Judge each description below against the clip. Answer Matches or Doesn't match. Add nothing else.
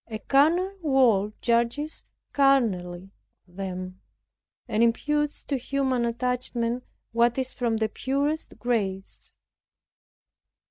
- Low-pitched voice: Doesn't match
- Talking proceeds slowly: Matches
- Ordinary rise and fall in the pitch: Matches